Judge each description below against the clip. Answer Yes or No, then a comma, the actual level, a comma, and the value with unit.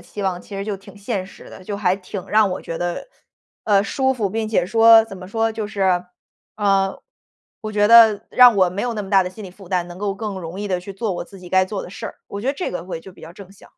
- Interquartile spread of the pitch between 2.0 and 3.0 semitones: Yes, average, 2.7 semitones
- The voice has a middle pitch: No, high, 200 Hz